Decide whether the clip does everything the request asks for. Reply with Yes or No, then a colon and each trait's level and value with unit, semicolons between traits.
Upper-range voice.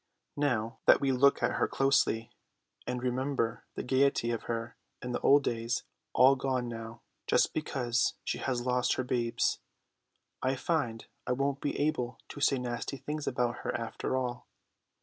No: low, 125 Hz